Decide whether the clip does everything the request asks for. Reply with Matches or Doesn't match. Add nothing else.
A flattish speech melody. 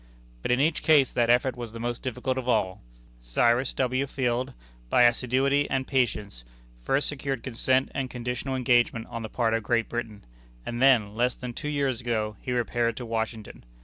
Matches